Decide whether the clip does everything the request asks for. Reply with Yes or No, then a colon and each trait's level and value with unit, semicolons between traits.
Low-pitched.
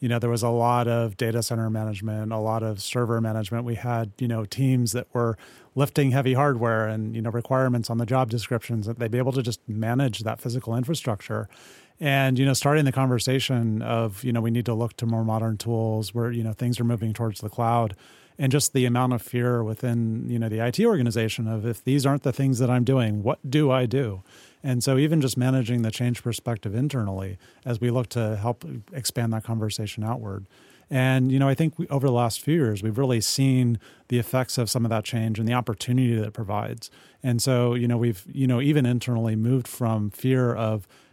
Yes: low, 120 Hz